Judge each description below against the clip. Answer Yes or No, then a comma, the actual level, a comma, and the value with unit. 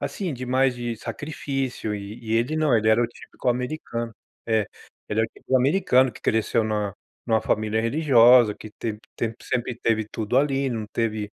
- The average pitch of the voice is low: Yes, low, 115 Hz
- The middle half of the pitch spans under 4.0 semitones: Yes, average, 2.9 semitones